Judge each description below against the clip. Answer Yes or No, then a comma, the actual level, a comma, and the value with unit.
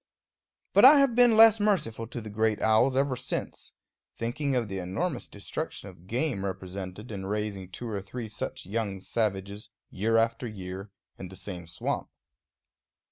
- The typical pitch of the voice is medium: No, low, 110 Hz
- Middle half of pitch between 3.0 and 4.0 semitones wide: No, average, 4.4 semitones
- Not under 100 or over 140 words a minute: No, average, 160 wpm